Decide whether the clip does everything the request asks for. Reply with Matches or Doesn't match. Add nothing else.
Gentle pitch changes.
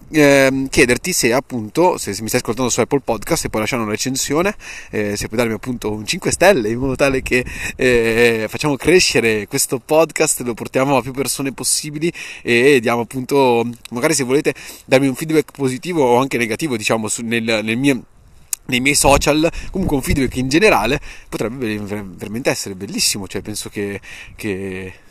Doesn't match